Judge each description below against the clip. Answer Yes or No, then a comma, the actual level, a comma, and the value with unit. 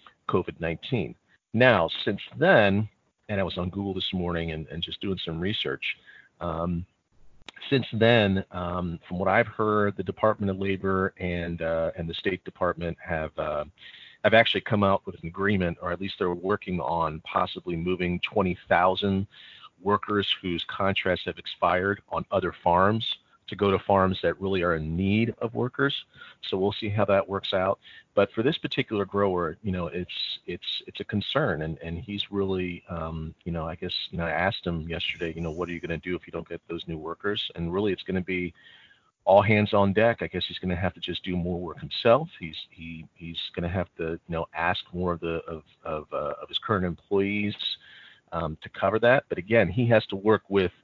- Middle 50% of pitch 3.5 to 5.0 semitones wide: No, average, 3.0 semitones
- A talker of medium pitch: No, very low, 90 Hz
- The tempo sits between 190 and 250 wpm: Yes, fast, 205 wpm